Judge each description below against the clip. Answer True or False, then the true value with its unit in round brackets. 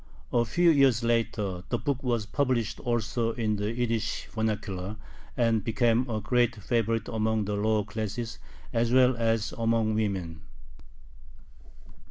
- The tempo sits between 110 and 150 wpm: True (135 wpm)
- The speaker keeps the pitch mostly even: True (1.9 semitones)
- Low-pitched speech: True (115 Hz)